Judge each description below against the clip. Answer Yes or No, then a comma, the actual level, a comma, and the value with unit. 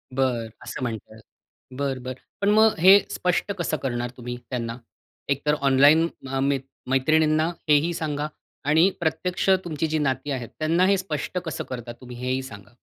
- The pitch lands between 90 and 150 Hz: Yes, medium, 140 Hz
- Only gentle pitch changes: No, average, 4.1 semitones